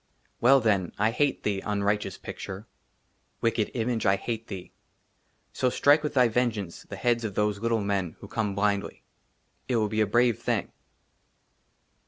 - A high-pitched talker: No, low, 110 Hz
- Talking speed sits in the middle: Yes, average, 160 wpm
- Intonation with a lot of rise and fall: No, average, 2.9 semitones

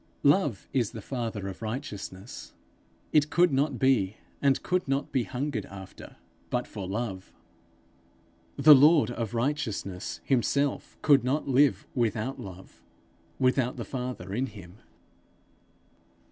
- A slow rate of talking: Yes, slow, 125 wpm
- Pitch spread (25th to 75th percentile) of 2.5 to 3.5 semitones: No, average, 5.0 semitones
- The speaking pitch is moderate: No, low, 125 Hz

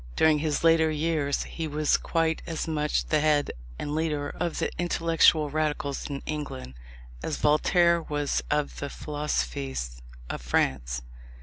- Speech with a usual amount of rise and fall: No, narrow, 2.1 semitones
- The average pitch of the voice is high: No, medium, 150 Hz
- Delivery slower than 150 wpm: Yes, average, 140 wpm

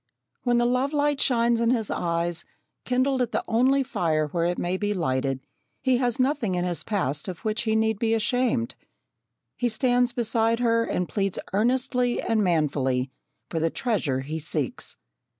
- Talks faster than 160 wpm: Yes, average, 170 wpm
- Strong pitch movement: Yes, wide, 6.3 semitones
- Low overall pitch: No, high, 220 Hz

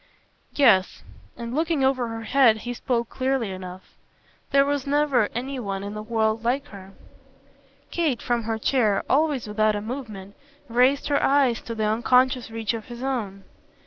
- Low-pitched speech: No, high, 235 Hz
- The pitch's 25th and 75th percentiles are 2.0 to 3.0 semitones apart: No, average, 3.8 semitones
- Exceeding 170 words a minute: No, average, 165 wpm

